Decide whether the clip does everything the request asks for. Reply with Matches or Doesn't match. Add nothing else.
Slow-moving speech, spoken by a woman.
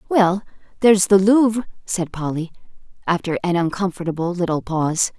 Matches